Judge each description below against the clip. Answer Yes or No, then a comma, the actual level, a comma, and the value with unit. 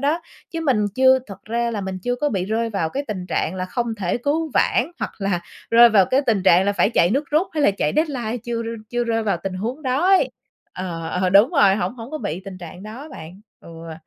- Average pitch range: No, wide, 5.7 semitones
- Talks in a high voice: Yes, high, 220 Hz